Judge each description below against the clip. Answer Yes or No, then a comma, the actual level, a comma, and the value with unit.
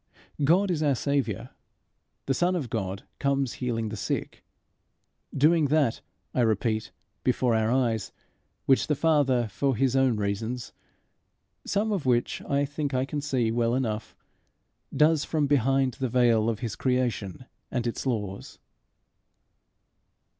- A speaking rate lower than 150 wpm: Yes, average, 140 wpm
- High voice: No, low, 130 Hz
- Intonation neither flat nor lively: Yes, average, 3.8 semitones